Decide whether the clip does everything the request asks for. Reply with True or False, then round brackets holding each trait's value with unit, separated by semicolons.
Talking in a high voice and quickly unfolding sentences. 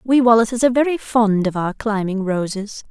False (220 Hz; 185 wpm)